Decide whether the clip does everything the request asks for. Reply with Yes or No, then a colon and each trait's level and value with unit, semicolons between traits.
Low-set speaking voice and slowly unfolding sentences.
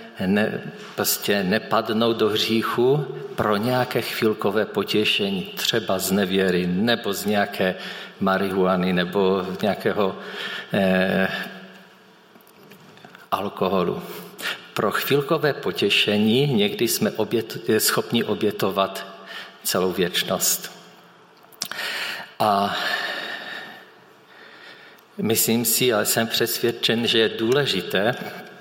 Yes: low, 115 Hz; slow, 85 wpm